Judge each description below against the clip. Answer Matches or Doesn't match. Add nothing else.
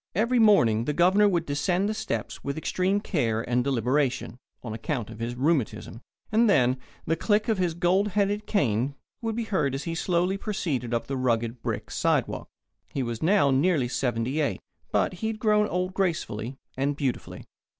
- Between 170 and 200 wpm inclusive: Matches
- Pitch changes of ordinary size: Doesn't match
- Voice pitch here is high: Doesn't match